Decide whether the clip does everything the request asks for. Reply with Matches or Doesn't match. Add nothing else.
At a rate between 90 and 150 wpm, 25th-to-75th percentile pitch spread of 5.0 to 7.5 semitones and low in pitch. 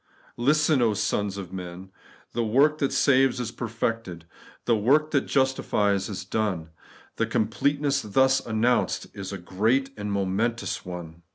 Matches